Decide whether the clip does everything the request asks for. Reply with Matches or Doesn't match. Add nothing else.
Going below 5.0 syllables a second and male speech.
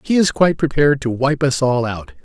Doesn't match